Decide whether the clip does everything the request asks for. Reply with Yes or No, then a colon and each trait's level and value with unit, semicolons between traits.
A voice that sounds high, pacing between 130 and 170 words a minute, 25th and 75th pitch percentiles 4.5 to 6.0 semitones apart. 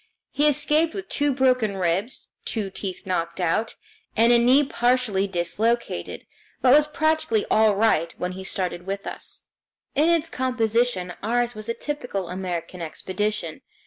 Yes: high, 220 Hz; average, 150 wpm; wide, 5.6 semitones